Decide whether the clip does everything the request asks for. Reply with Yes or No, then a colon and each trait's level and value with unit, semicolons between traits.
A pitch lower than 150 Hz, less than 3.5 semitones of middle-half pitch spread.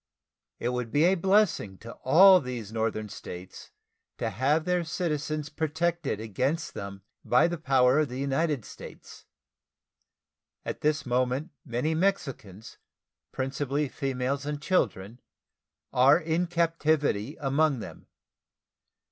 No: medium, 140 Hz; average, 4.5 semitones